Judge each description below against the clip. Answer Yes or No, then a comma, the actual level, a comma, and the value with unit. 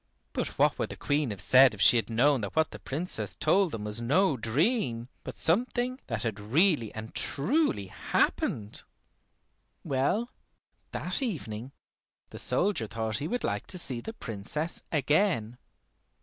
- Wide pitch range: Yes, wide, 8.3 semitones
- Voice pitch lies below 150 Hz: Yes, low, 135 Hz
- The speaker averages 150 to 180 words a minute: Yes, average, 155 wpm